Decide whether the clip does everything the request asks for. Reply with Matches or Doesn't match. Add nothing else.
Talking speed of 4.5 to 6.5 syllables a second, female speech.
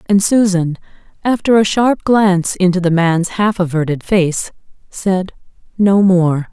Doesn't match